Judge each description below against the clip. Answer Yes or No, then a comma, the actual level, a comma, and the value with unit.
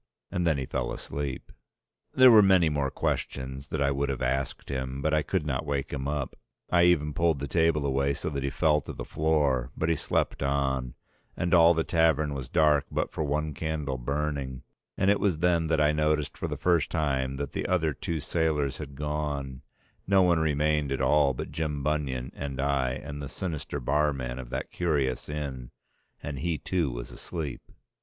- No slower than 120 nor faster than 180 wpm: No, average, 195 wpm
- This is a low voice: Yes, very low, 75 Hz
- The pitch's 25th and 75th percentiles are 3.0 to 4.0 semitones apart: No, narrow, 2.6 semitones